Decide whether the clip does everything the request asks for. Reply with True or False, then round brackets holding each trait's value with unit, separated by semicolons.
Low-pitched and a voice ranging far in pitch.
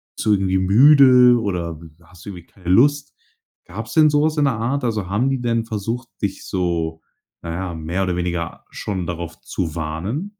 True (95 Hz; 6.1 semitones)